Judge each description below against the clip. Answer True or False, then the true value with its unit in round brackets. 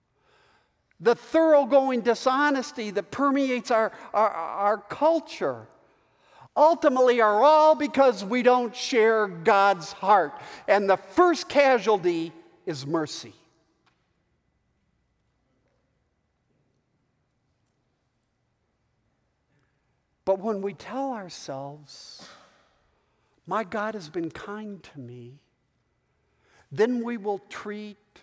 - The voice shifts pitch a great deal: True (7.7 semitones)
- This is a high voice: True (210 Hz)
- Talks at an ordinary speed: False (85 wpm)